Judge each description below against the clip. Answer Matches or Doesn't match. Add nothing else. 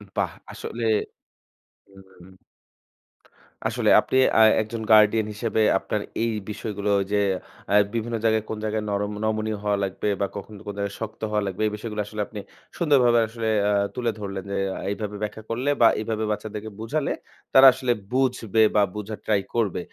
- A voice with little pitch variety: Matches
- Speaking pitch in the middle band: Doesn't match